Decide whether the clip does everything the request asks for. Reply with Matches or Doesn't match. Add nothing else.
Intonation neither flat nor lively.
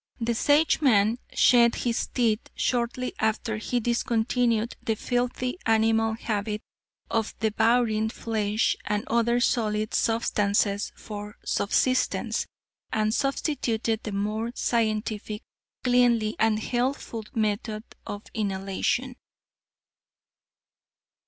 Doesn't match